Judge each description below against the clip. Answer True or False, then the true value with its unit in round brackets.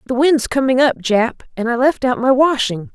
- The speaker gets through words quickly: True (225 wpm)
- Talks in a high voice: True (250 Hz)